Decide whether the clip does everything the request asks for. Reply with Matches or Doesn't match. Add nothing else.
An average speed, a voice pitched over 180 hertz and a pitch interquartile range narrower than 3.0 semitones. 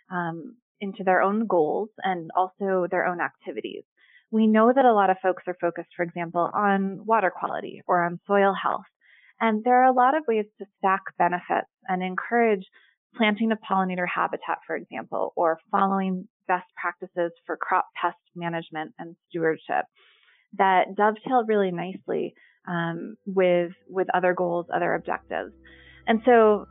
Doesn't match